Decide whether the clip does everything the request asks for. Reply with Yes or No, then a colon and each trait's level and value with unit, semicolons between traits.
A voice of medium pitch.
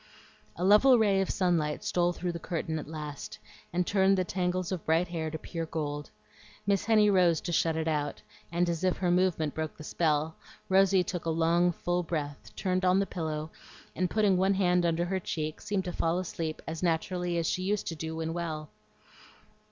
Yes: medium, 175 Hz